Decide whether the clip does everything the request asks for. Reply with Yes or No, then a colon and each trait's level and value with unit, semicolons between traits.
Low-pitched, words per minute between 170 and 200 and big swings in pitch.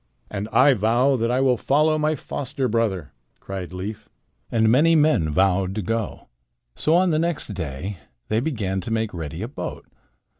Yes: low, 115 Hz; average, 175 wpm; wide, 6.3 semitones